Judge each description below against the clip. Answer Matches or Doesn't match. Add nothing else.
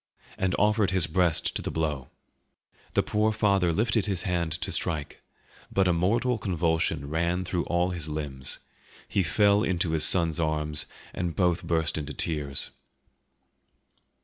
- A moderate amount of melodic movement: Matches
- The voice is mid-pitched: Doesn't match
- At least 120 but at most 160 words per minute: Matches